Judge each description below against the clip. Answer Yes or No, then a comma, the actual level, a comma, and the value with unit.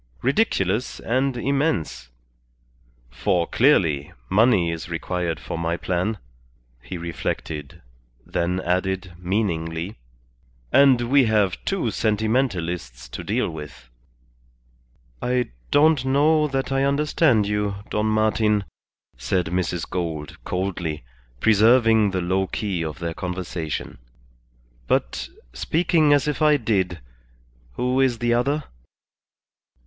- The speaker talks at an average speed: No, slow, 110 wpm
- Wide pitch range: Yes, wide, 6.8 semitones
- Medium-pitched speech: No, low, 100 Hz